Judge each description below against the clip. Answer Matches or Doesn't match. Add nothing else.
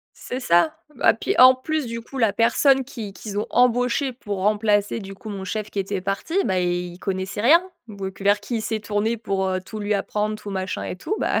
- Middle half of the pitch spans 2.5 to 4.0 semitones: Matches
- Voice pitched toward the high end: Matches